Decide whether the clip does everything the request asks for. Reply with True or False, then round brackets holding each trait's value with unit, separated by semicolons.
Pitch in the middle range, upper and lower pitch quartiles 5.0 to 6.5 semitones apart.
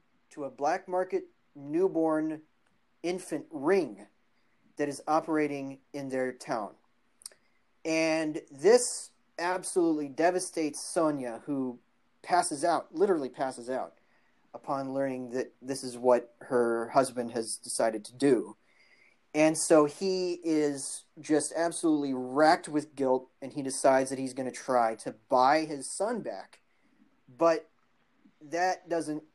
False (150 Hz; 4.2 semitones)